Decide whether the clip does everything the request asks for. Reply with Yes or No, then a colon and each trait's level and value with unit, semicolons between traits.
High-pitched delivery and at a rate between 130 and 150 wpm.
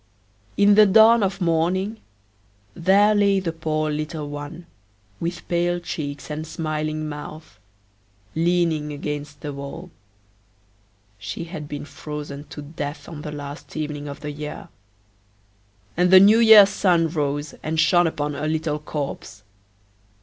No: medium, 155 Hz; slow, 135 wpm